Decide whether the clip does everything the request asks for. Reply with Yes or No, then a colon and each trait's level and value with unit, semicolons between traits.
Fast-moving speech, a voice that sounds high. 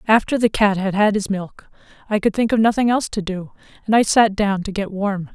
Yes: fast, 245 wpm; high, 205 Hz